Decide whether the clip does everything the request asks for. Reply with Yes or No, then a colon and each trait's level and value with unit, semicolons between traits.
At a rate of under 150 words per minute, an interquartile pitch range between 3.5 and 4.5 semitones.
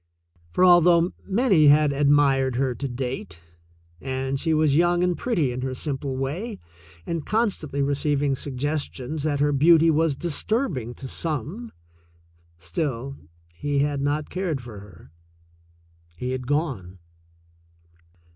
Yes: slow, 135 wpm; average, 3.9 semitones